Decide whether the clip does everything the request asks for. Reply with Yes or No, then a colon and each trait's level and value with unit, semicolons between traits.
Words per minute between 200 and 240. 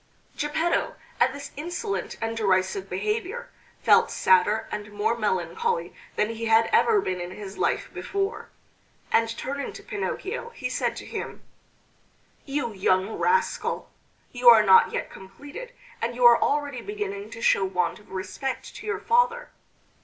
No: average, 150 wpm